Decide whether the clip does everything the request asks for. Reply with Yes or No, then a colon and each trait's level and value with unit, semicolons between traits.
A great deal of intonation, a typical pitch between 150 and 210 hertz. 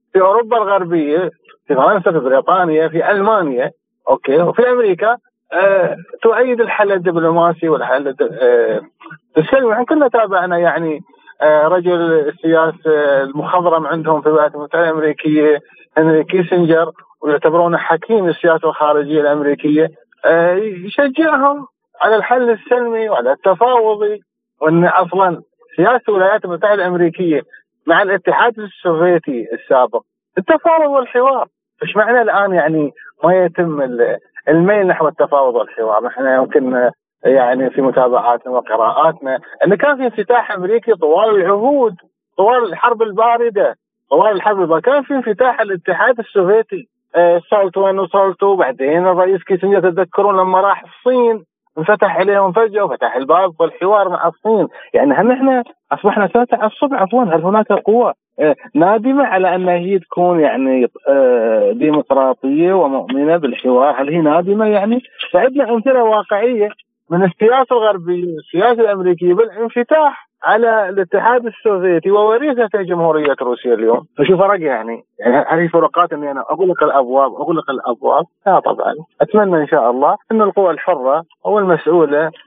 Yes: wide, 6.5 semitones; high, 190 Hz